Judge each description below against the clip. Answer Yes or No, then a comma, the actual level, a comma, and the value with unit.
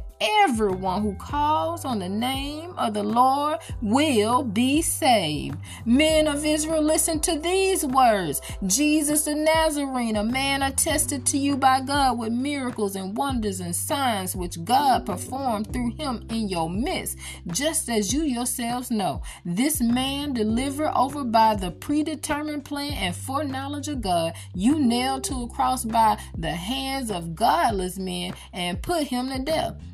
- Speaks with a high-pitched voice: Yes, very high, 255 Hz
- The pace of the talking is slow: No, average, 150 wpm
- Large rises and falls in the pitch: Yes, wide, 5.9 semitones